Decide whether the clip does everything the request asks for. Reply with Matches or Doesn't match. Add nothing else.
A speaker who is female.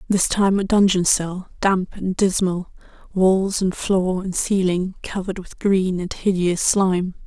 Matches